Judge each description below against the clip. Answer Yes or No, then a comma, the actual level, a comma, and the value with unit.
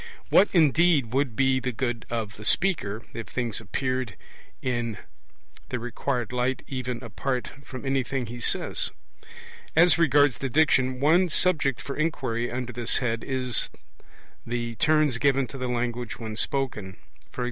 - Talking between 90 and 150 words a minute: Yes, average, 145 wpm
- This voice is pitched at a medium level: No, low, 125 Hz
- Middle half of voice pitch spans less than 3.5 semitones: Yes, average, 2.8 semitones